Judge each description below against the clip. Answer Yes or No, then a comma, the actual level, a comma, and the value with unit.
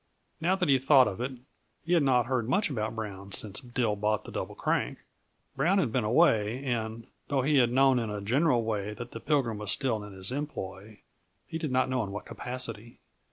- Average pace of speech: No, fast, 210 wpm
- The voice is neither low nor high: No, low, 120 Hz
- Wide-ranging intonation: No, average, 4.1 semitones